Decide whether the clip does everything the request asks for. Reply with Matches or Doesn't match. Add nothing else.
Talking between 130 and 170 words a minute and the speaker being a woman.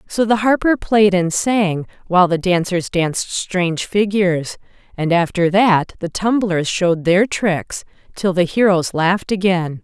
Matches